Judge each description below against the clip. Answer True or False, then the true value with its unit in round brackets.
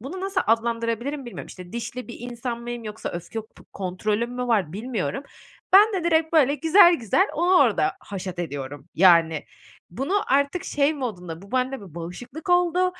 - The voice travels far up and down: True (7.7 semitones)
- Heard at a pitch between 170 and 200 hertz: False (240 Hz)